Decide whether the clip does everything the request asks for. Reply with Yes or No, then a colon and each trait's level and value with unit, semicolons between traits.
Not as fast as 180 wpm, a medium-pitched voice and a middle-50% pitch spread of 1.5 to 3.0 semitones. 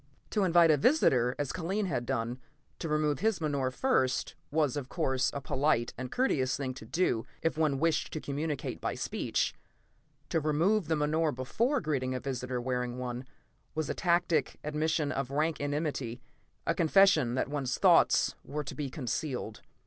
No: average, 170 wpm; medium, 145 Hz; average, 3.9 semitones